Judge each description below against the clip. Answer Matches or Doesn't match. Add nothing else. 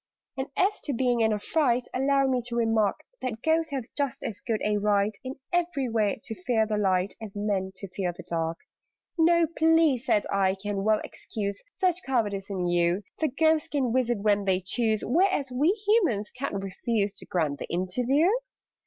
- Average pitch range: Doesn't match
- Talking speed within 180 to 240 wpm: Matches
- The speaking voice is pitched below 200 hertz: Doesn't match